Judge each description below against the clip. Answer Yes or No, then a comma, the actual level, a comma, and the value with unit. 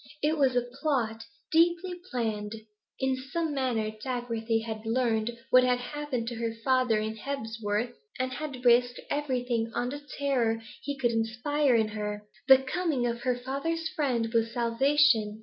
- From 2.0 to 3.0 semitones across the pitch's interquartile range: No, average, 3.4 semitones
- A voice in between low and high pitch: No, high, 245 Hz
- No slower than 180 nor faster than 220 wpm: No, average, 155 wpm